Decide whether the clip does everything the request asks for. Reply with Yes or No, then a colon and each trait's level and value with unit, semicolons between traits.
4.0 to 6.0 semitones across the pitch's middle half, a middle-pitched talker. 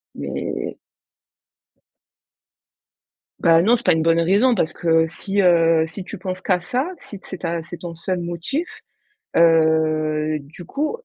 No: average, 2.8 semitones; medium, 170 Hz